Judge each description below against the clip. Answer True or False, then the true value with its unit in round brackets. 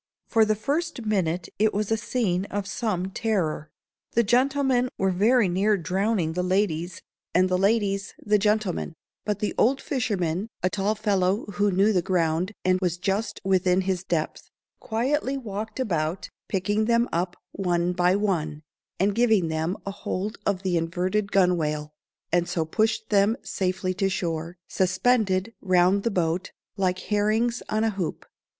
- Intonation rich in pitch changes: False (3.2 semitones)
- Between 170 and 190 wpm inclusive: False (155 wpm)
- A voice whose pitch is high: True (195 Hz)